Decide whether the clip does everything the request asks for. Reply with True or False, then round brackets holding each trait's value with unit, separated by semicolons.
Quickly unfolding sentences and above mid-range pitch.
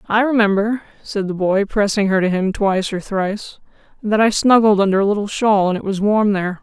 True (215 wpm; 205 Hz)